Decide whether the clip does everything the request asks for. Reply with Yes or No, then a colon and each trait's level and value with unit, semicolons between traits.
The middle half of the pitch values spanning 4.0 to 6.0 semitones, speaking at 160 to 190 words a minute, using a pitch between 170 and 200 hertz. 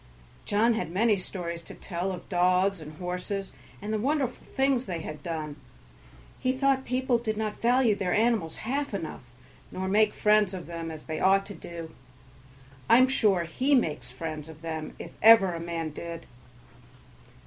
Yes: wide, 5.4 semitones; average, 170 wpm; high, 190 Hz